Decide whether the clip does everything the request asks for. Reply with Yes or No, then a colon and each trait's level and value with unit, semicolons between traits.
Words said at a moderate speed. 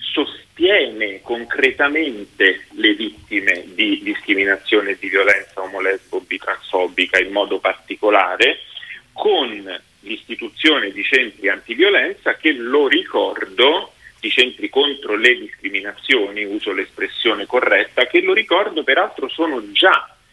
No: slow, 105 wpm